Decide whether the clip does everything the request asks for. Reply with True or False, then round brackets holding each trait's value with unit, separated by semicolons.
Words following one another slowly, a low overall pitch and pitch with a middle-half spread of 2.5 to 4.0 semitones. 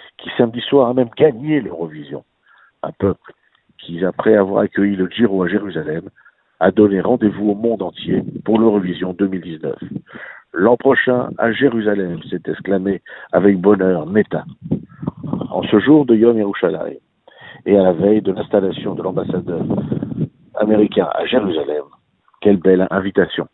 True (140 wpm; 105 Hz; 3.5 semitones)